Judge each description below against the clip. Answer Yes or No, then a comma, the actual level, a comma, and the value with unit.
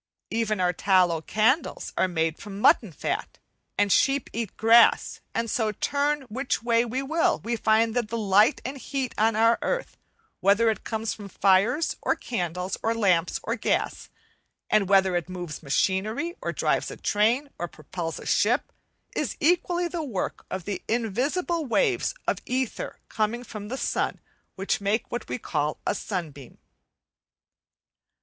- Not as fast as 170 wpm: Yes, average, 160 wpm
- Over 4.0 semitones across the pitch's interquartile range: Yes, average, 4.7 semitones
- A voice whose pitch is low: No, high, 220 Hz